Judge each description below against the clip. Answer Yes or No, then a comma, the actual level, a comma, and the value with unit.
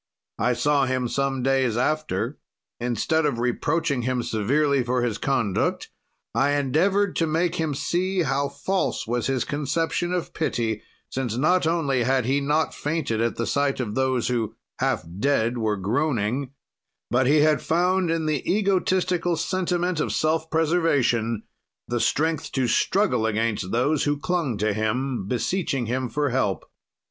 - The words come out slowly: No, average, 155 wpm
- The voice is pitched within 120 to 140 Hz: Yes, low, 135 Hz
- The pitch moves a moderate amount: Yes, average, 5.0 semitones